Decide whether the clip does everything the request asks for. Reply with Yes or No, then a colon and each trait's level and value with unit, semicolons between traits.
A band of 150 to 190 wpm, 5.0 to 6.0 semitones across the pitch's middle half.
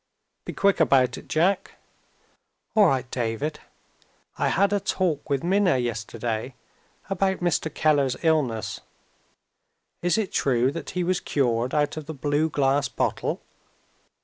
No: slow, 135 wpm; wide, 5.5 semitones